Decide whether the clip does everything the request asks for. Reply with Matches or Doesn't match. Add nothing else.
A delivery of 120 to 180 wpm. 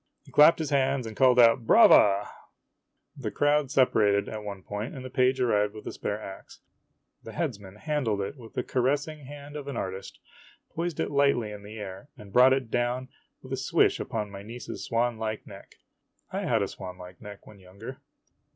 Doesn't match